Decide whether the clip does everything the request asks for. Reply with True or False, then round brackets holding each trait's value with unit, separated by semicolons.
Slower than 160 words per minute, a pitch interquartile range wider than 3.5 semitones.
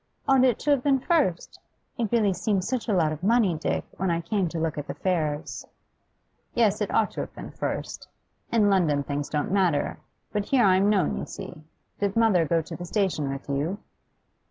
False (205 wpm; 5.1 semitones)